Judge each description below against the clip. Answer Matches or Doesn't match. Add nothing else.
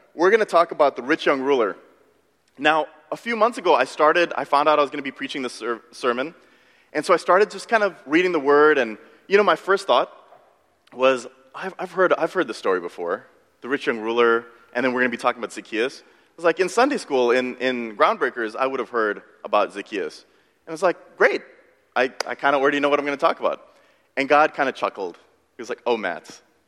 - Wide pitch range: Matches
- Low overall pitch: Doesn't match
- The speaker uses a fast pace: Matches